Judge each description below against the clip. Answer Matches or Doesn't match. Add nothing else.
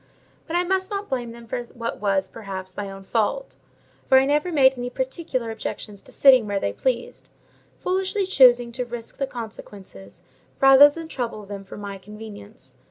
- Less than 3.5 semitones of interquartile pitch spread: Doesn't match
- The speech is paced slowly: Doesn't match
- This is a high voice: Matches